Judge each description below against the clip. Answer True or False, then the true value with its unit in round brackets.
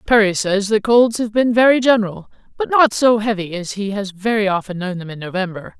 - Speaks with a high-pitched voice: True (210 Hz)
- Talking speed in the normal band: False (220 wpm)